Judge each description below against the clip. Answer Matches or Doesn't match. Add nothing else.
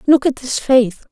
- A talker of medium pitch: Doesn't match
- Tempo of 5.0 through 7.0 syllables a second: Doesn't match